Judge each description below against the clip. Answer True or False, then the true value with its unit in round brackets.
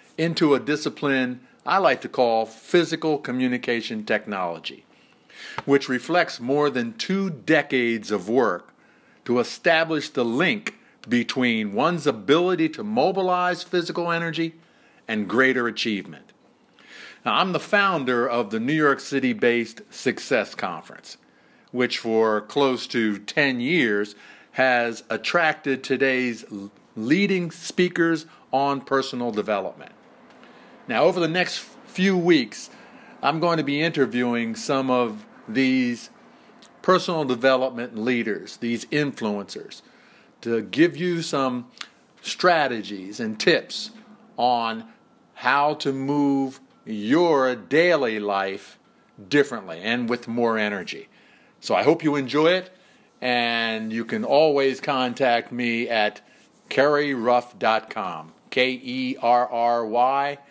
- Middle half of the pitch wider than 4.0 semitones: True (5.4 semitones)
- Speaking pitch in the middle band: False (130 Hz)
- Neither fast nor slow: False (115 wpm)